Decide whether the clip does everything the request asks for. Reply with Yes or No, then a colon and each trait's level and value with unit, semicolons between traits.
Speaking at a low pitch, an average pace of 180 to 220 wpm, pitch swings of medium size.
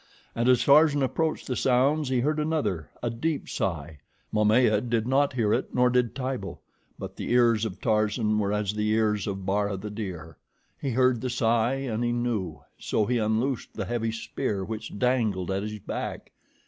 Yes: low, 115 Hz; average, 185 wpm; average, 3.3 semitones